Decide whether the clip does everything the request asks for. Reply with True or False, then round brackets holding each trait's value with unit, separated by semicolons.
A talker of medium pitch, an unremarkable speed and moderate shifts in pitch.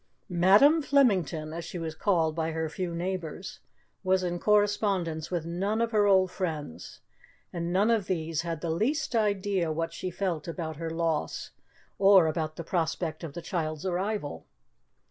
True (175 Hz; 165 wpm; 3.4 semitones)